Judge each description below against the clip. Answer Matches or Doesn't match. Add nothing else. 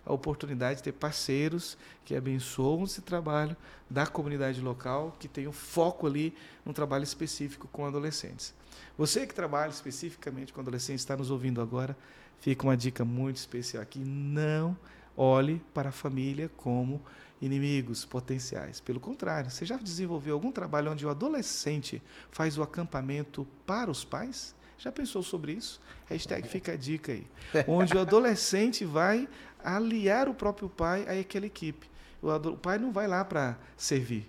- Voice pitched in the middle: Matches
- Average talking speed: Matches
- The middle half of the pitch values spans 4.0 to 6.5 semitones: Matches